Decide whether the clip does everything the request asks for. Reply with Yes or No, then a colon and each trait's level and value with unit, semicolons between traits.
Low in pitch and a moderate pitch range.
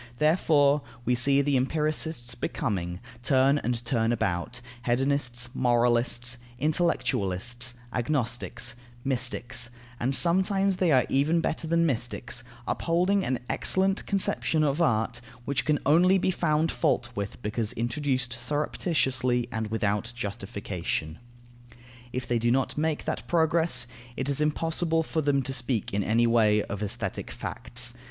Yes: low, 130 Hz; average, 4.5 semitones